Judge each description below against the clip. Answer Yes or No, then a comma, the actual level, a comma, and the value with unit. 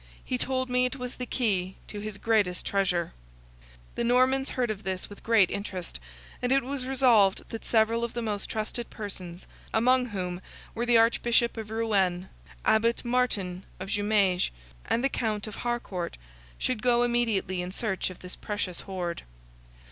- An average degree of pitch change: Yes, average, 4.1 semitones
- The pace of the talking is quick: No, average, 165 wpm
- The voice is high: Yes, high, 220 Hz